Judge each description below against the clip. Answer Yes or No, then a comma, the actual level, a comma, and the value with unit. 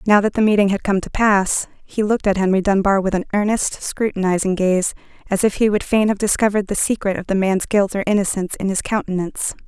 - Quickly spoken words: Yes, fast, 225 wpm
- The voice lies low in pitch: No, high, 200 Hz